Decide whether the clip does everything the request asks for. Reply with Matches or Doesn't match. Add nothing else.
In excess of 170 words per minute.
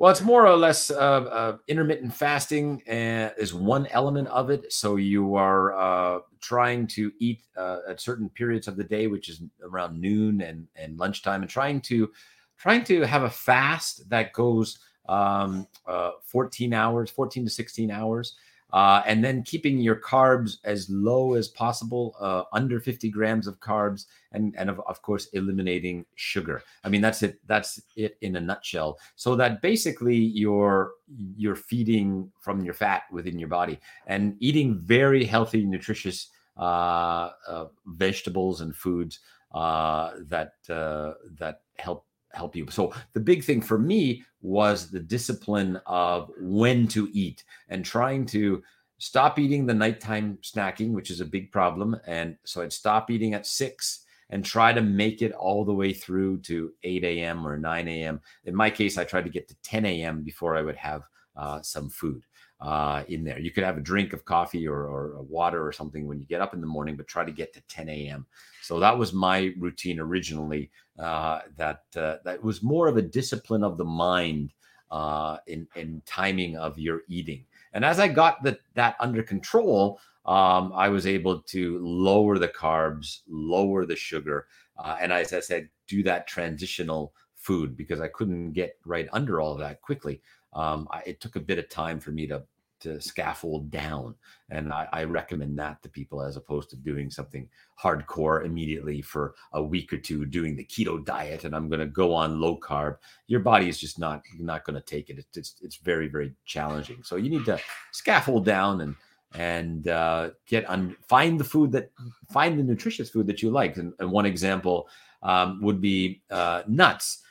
Matches